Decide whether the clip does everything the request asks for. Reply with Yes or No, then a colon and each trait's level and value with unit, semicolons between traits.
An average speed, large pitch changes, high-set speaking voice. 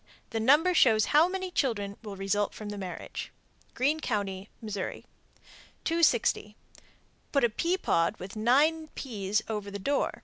Yes: average, 145 wpm; wide, 6.5 semitones; high, 220 Hz